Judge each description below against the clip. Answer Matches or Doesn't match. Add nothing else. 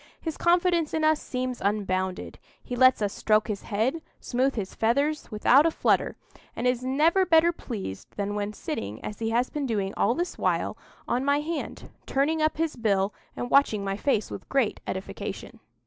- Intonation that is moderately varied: Doesn't match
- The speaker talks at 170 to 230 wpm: Matches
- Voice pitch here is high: Matches